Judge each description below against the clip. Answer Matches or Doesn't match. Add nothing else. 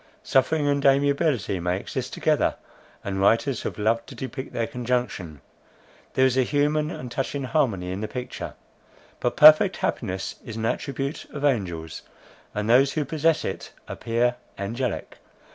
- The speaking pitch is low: Matches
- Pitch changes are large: Doesn't match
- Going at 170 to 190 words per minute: Doesn't match